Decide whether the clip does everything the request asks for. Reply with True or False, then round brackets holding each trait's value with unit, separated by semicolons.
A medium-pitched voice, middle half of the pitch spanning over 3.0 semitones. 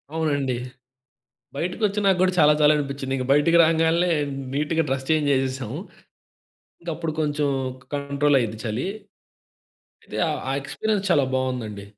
True (145 Hz; 3.5 semitones)